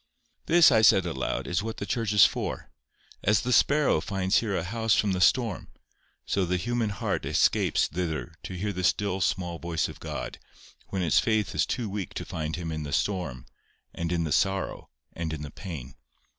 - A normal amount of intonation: Yes, average, 4.0 semitones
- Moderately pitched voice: No, very low, 95 Hz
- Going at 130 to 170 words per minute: No, average, 200 wpm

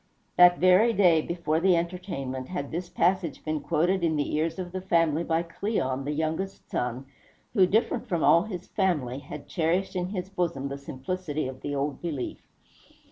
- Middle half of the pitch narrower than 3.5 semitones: No, average, 4.0 semitones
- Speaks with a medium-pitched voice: Yes, medium, 170 Hz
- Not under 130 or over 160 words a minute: No, average, 180 wpm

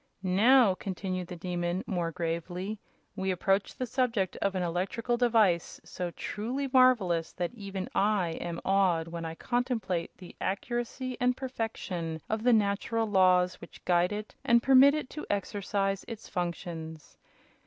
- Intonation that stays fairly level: No, average, 4.6 semitones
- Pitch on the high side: Yes, high, 195 Hz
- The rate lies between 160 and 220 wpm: No, average, 145 wpm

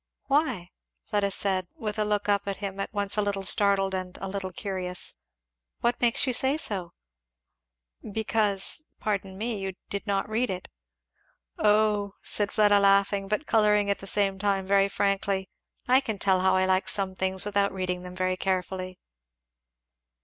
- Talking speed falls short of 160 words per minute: No, average, 165 wpm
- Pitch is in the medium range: No, high, 200 Hz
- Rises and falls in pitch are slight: Yes, narrow, 1.7 semitones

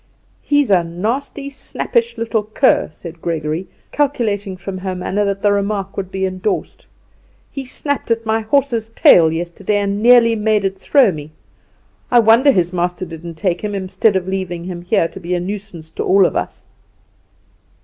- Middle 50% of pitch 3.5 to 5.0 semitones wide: Yes, average, 4.0 semitones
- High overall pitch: Yes, high, 195 Hz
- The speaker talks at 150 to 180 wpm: Yes, average, 170 wpm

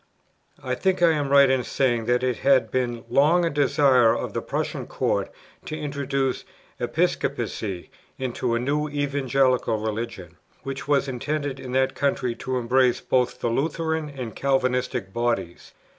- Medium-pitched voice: No, low, 130 Hz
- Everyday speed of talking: Yes, average, 150 wpm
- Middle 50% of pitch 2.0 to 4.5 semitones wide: Yes, average, 2.8 semitones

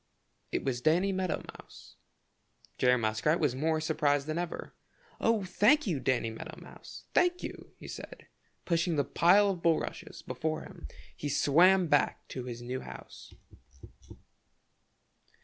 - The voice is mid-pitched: Yes, medium, 155 Hz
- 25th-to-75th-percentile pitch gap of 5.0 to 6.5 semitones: Yes, wide, 5.6 semitones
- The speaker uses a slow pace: No, average, 145 wpm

